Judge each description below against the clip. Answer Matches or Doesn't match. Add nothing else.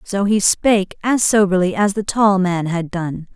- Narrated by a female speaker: Matches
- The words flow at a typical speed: Matches